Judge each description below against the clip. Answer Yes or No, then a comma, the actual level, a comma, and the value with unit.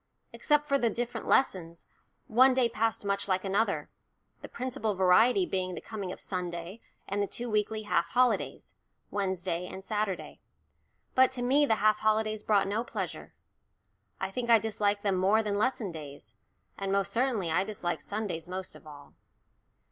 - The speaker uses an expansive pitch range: No, average, 3.6 semitones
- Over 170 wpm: No, average, 165 wpm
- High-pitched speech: Yes, high, 205 Hz